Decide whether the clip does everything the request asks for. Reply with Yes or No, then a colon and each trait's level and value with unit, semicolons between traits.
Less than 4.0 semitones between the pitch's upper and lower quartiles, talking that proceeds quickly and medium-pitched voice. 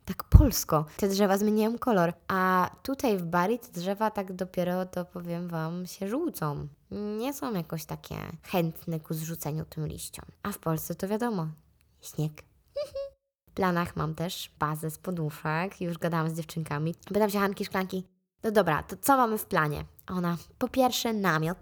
No: average, 4.3 semitones; fast, 165 wpm; medium, 180 Hz